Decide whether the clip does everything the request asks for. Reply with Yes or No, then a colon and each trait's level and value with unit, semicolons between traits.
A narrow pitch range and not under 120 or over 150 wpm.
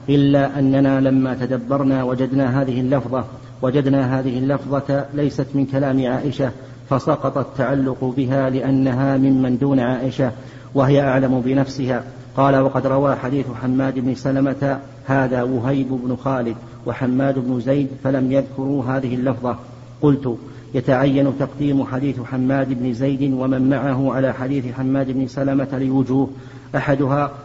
Yes: narrow, 1.0 semitones; average, 125 wpm